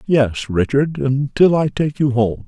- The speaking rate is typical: Yes, average, 170 wpm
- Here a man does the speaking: Yes, male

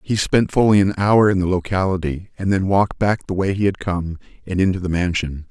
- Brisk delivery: Yes, fast, 230 wpm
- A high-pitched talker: No, very low, 95 Hz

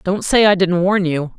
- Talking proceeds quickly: Yes, fast, 260 wpm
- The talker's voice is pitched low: No, medium, 185 Hz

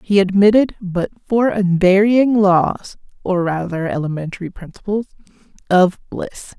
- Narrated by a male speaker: No, female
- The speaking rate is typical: No, slow, 110 wpm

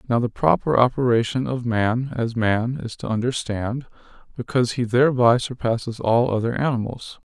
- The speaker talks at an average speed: Yes, average, 150 wpm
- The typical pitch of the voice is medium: No, low, 120 Hz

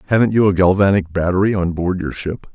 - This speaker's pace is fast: Yes, fast, 215 wpm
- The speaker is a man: Yes, male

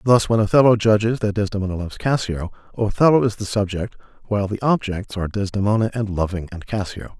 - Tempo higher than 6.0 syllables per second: Yes, 6.3 syllables/s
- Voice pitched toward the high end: No, low, 105 Hz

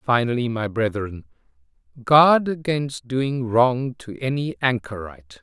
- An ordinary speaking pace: No, slow, 110 wpm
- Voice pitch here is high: No, low, 120 Hz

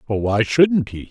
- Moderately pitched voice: No, low, 120 Hz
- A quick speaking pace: No, average, 165 wpm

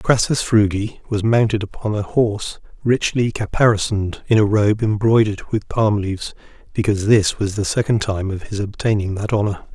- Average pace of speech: Yes, average, 165 wpm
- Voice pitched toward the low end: Yes, low, 105 Hz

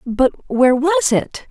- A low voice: No, very high, 280 Hz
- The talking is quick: No, average, 160 wpm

